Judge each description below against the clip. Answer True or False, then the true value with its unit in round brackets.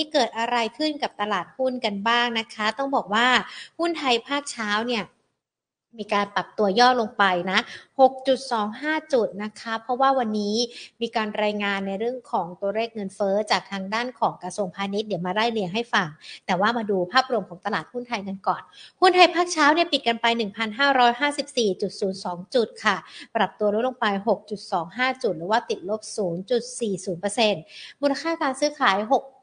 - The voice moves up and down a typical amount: True (4.0 semitones)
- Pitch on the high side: True (225 Hz)